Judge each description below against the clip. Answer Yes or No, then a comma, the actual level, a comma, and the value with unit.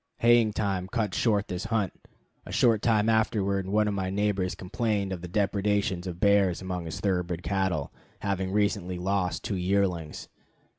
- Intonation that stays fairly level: Yes, narrow, 2.3 semitones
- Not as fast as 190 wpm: Yes, average, 160 wpm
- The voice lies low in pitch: Yes, low, 100 Hz